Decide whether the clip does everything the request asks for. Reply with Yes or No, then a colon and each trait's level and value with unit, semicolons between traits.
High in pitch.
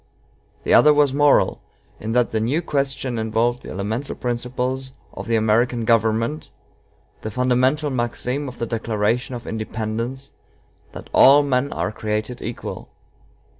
No: low, 120 Hz